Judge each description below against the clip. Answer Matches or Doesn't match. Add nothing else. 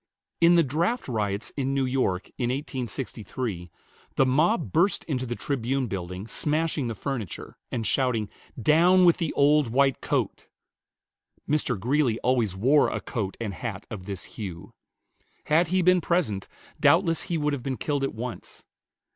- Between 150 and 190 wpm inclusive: Matches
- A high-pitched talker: Doesn't match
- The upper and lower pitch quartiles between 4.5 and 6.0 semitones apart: Matches